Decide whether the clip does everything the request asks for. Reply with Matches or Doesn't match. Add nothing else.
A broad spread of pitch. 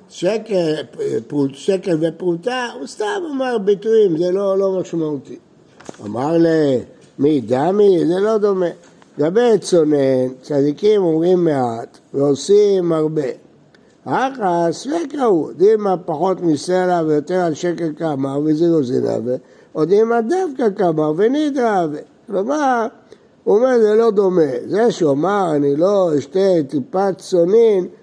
Matches